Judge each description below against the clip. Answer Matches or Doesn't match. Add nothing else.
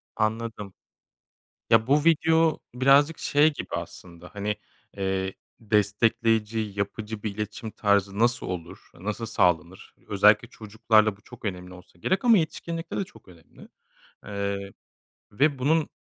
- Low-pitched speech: Matches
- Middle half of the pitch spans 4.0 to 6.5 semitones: Matches